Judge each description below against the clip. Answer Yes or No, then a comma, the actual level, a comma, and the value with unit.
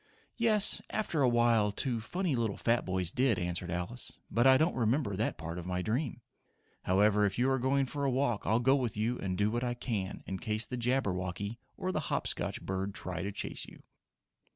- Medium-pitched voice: No, low, 115 Hz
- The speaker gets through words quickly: Yes, fast, 210 wpm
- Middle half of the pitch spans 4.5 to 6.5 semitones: Yes, average, 5.2 semitones